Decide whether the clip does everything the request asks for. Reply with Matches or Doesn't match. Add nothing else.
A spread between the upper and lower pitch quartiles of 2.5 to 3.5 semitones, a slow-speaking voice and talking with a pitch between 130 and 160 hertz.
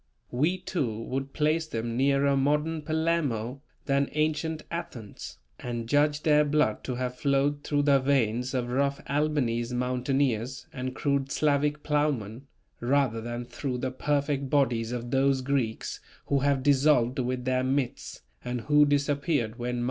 Doesn't match